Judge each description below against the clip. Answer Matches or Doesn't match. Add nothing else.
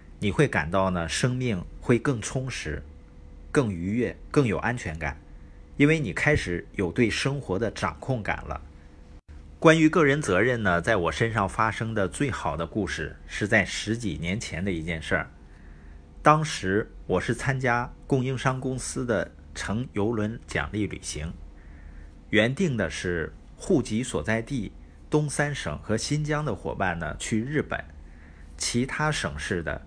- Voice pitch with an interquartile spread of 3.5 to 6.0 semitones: Doesn't match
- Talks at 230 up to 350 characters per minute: Doesn't match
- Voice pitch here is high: Doesn't match